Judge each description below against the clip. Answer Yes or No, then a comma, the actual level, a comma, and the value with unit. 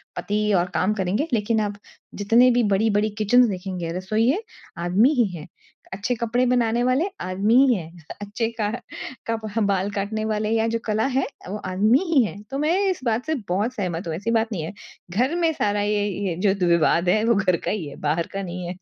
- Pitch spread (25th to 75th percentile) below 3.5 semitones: No, average, 3.8 semitones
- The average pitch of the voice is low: No, high, 210 Hz